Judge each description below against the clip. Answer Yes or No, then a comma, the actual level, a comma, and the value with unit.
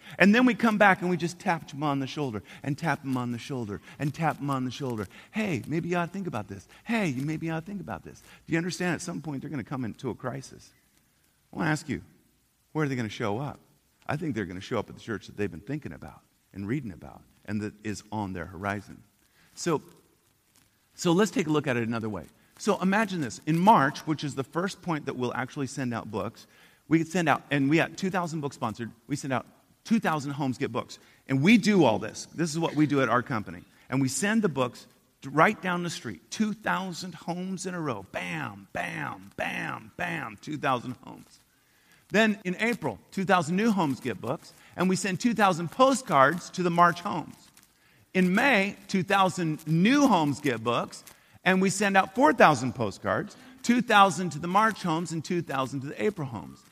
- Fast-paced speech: Yes, fast, 220 wpm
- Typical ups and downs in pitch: No, wide, 6.3 semitones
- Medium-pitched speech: Yes, medium, 155 Hz